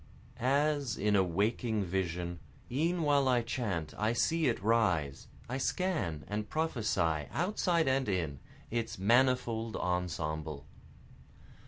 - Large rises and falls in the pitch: Yes, wide, 7.0 semitones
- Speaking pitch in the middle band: No, low, 110 Hz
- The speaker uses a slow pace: Yes, slow, 120 wpm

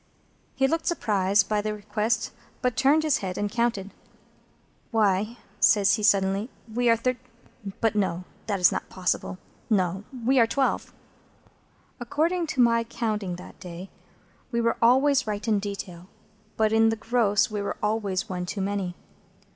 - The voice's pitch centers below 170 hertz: No, high, 215 Hz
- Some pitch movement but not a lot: Yes, average, 3.3 semitones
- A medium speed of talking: Yes, average, 155 wpm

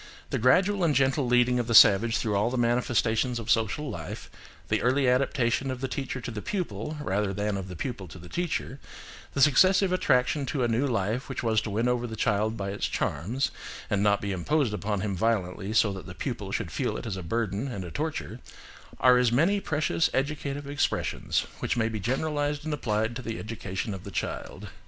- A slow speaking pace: No, fast, 205 wpm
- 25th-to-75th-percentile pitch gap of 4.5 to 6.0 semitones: Yes, average, 4.8 semitones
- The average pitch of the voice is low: Yes, low, 120 Hz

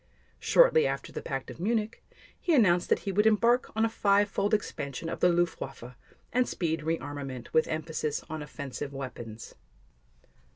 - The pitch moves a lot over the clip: Yes, wide, 6.8 semitones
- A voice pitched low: No, medium, 165 Hz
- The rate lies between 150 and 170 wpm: Yes, average, 160 wpm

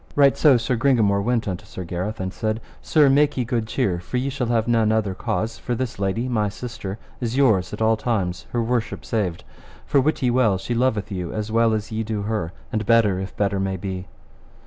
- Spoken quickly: Yes, fast, 220 wpm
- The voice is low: Yes, low, 110 Hz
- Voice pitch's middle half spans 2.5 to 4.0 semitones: Yes, average, 3.5 semitones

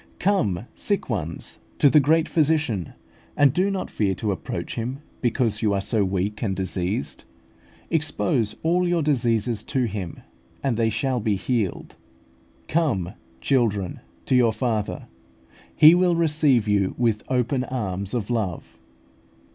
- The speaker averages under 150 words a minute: Yes, average, 140 wpm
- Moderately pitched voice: No, low, 115 Hz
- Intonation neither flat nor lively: No, wide, 6.1 semitones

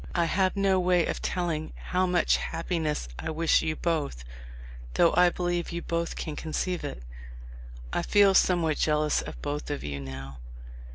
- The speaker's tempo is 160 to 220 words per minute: Yes, average, 175 wpm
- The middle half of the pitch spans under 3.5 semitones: Yes, average, 2.9 semitones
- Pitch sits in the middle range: Yes, medium, 165 Hz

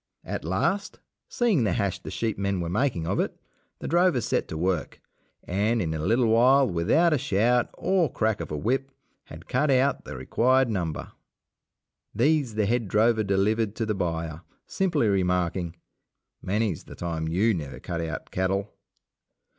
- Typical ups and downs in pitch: No, wide, 6.2 semitones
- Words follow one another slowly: No, average, 165 wpm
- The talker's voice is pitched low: Yes, low, 105 Hz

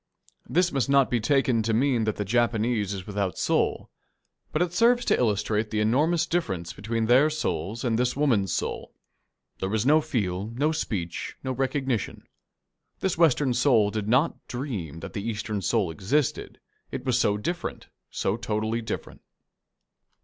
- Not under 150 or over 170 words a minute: Yes, average, 160 wpm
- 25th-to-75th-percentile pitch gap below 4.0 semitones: No, average, 4.8 semitones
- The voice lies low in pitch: Yes, low, 115 Hz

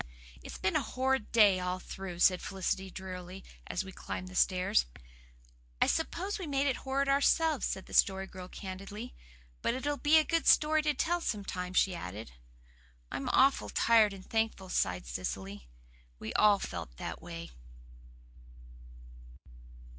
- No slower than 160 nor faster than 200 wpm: No, average, 150 wpm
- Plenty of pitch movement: Yes, wide, 6.8 semitones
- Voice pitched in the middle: No, high, 195 Hz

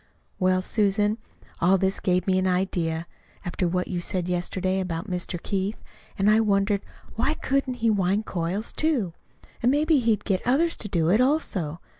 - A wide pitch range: No, average, 3.5 semitones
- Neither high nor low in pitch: No, high, 195 Hz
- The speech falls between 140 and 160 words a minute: No, average, 170 wpm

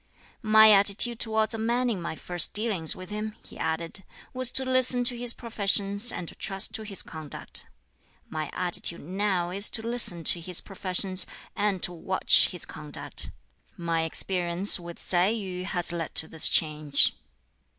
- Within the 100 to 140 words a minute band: No, average, 165 wpm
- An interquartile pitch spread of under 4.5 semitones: Yes, average, 4.1 semitones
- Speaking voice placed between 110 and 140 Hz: No, high, 190 Hz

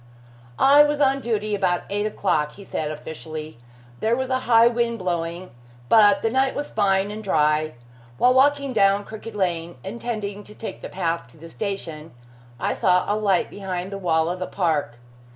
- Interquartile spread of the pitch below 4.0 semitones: No, average, 5.1 semitones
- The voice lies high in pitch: Yes, high, 200 Hz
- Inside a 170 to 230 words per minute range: Yes, average, 180 wpm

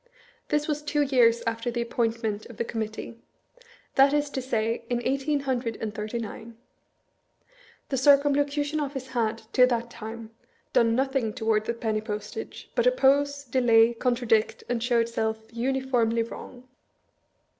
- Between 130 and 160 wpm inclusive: Yes, average, 145 wpm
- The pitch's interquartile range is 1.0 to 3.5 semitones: Yes, average, 3.1 semitones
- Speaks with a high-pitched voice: Yes, high, 240 Hz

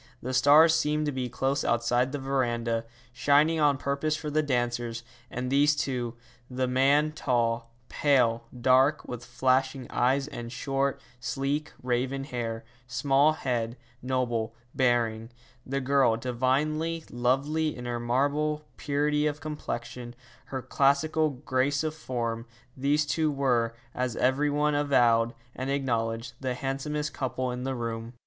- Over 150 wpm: No, average, 140 wpm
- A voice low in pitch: Yes, low, 130 Hz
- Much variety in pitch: No, average, 3.1 semitones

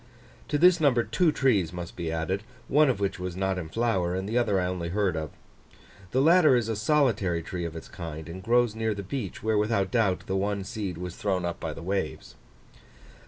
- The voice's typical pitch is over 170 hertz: No, low, 100 Hz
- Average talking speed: No, fast, 215 wpm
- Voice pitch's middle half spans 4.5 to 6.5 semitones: Yes, average, 4.8 semitones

